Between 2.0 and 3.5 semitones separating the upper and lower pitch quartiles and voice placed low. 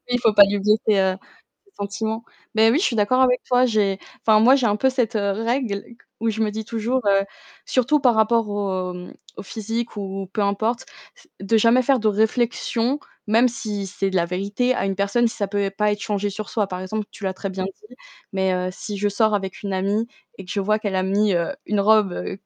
No: average, 2.8 semitones; high, 210 Hz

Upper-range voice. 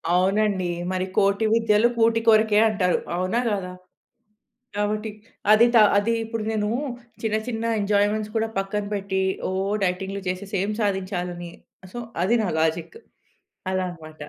Yes: high, 205 Hz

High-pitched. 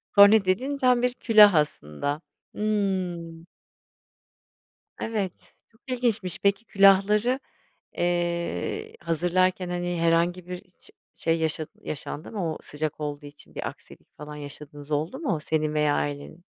No: medium, 175 Hz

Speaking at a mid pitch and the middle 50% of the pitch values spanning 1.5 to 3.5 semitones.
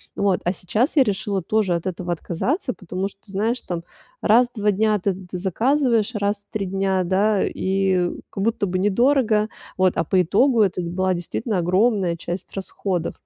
No: high, 195 Hz; average, 2.9 semitones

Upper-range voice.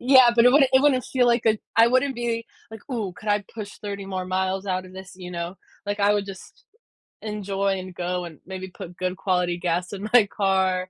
Yes: high, 195 Hz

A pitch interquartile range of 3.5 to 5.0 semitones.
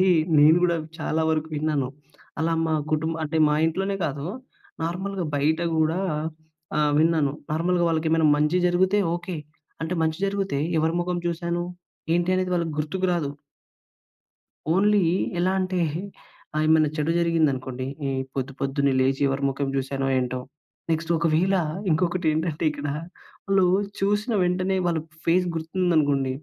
No: average, 3.1 semitones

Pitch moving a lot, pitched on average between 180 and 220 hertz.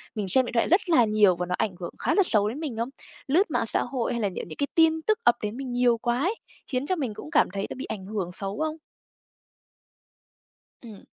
No: wide, 5.8 semitones; high, 240 Hz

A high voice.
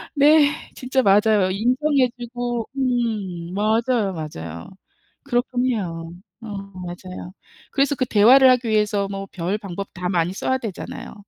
Yes: high, 215 Hz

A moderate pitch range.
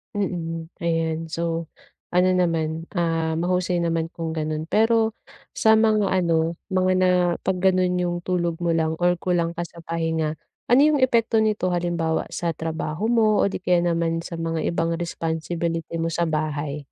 No: narrow, 2.0 semitones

